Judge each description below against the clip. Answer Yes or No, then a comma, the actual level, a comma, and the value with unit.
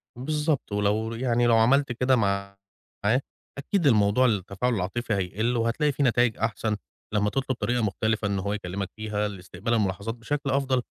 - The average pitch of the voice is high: No, low, 115 Hz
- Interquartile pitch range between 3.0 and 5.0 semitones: Yes, average, 3.7 semitones